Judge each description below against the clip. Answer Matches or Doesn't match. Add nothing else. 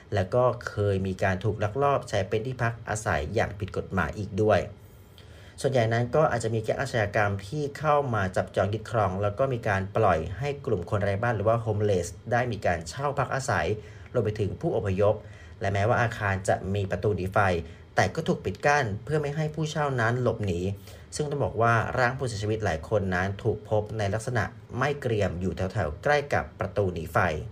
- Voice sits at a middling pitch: Doesn't match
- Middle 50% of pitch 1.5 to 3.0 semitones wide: Doesn't match